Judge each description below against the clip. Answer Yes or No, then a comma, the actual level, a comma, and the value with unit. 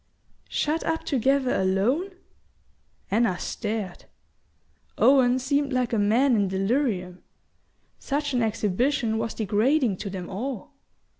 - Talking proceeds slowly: Yes, slow, 115 wpm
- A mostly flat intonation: No, average, 5.2 semitones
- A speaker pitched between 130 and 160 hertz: No, high, 235 Hz